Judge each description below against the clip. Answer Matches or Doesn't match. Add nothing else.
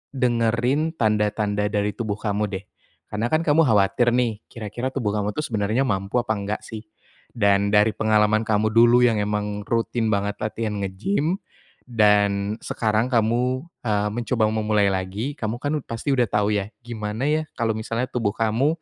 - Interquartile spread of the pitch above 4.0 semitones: Doesn't match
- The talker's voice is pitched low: Matches